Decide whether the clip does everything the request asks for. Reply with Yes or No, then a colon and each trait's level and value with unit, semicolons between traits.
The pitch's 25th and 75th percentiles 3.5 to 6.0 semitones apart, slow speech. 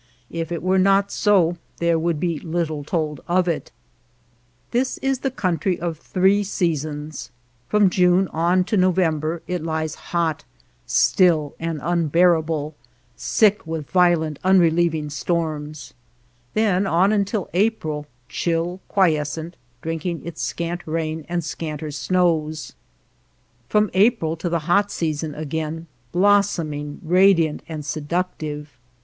No: average, 2.8 semitones; slow, 120 wpm